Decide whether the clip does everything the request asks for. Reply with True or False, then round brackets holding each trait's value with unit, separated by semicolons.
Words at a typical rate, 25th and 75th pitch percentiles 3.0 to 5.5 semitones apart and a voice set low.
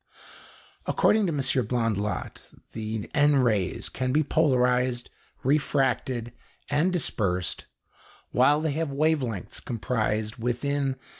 False (100 wpm; 4.2 semitones; 130 Hz)